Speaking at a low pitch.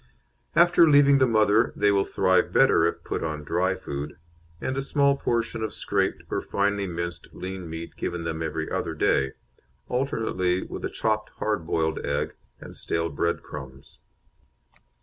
Yes: very low, 90 Hz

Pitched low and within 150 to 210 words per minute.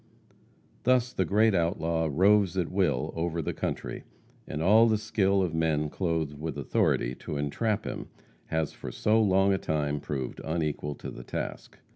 Yes: very low, 85 Hz; average, 165 wpm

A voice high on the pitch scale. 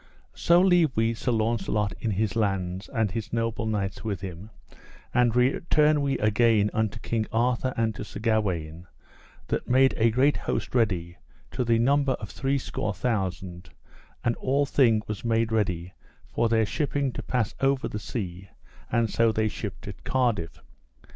No: low, 115 Hz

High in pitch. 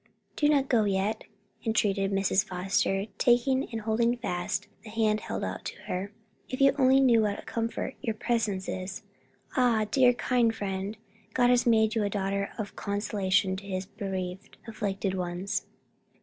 Yes: high, 210 Hz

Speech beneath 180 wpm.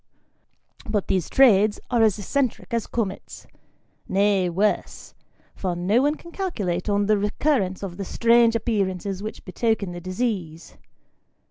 Yes: slow, 135 wpm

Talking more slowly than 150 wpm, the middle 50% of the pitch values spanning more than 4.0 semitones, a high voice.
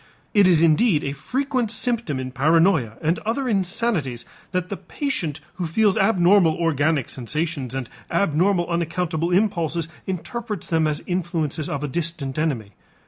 No: average, 140 wpm; average, 4.7 semitones; medium, 170 Hz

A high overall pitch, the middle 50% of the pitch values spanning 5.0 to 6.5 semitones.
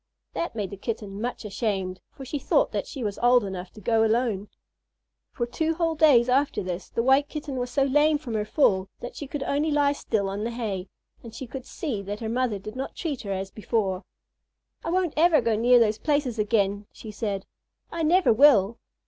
Yes: high, 235 Hz; wide, 5.6 semitones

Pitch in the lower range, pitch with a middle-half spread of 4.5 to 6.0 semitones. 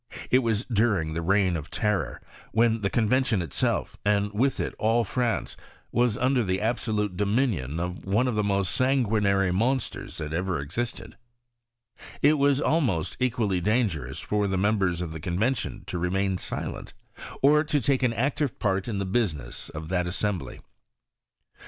Yes: low, 105 Hz; average, 4.8 semitones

